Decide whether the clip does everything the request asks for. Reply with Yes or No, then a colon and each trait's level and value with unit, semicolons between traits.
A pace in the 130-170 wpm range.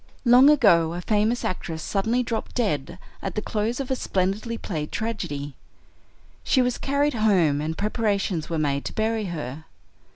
Yes: average, 160 wpm